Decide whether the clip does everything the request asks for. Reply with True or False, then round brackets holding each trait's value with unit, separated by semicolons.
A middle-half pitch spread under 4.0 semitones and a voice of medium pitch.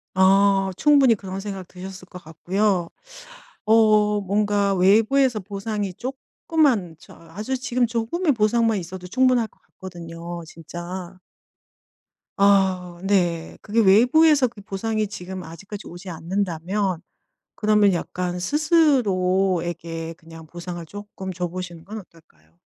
False (3.6 semitones; 195 Hz)